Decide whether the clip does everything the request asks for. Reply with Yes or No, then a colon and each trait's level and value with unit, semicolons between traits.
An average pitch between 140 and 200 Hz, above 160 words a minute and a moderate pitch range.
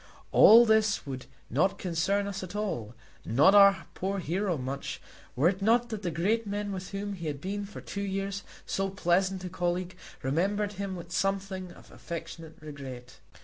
Yes: high, 190 Hz; average, 175 wpm; average, 3.1 semitones